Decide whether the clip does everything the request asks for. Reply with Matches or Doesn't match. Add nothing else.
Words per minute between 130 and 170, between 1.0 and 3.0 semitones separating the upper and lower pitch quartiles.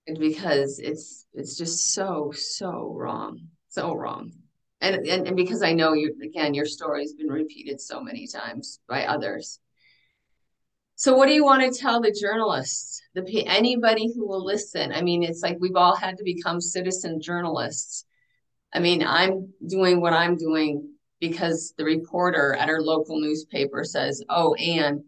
Doesn't match